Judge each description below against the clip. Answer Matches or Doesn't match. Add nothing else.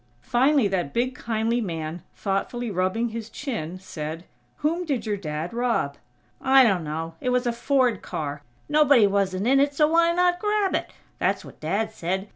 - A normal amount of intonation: Doesn't match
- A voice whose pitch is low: Doesn't match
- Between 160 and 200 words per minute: Matches